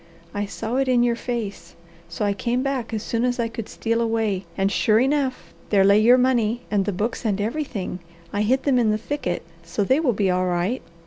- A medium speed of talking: No, fast, 220 wpm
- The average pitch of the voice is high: Yes, high, 225 Hz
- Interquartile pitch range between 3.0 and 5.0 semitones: Yes, average, 3.6 semitones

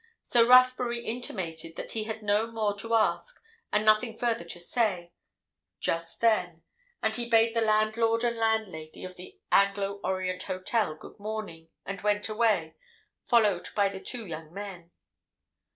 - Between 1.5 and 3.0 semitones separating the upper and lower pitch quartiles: No, average, 3.8 semitones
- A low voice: No, high, 210 Hz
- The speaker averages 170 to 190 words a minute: No, average, 150 wpm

